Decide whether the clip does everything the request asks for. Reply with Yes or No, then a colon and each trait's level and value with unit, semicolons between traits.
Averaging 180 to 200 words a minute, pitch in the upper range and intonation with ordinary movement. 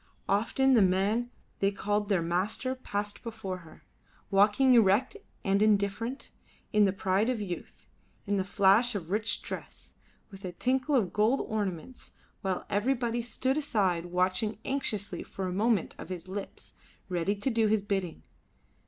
No: average, 155 wpm; high, 205 Hz; average, 3.3 semitones